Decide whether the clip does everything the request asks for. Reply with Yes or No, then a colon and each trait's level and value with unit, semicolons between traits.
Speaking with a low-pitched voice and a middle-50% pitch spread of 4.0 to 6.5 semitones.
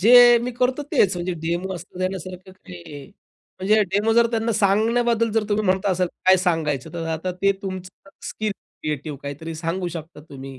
No: medium, 185 Hz; average, 4.6 semitones